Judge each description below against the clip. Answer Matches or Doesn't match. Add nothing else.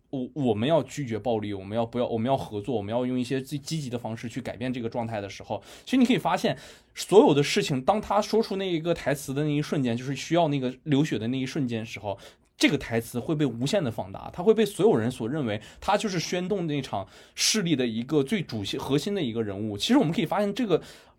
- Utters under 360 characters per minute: Doesn't match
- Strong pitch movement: Matches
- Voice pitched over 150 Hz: Doesn't match